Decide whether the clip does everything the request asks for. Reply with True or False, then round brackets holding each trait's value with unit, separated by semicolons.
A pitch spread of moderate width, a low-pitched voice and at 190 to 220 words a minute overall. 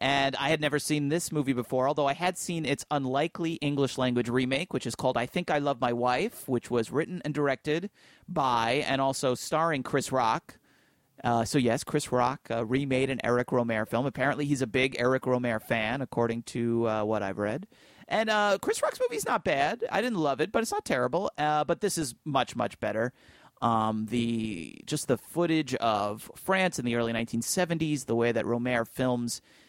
True (4.1 semitones; 130 Hz; 200 wpm)